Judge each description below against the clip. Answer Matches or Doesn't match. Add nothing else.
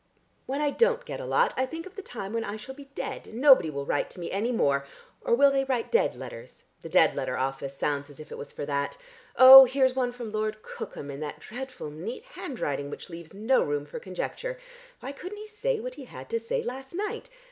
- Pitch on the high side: Matches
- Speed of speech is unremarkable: Doesn't match